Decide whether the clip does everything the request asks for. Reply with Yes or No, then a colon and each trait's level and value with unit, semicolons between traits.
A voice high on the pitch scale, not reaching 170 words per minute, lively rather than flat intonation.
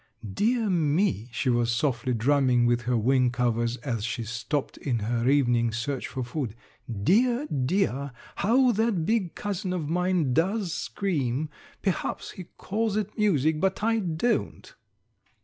No: medium, 145 Hz; average, 145 wpm; wide, 8.2 semitones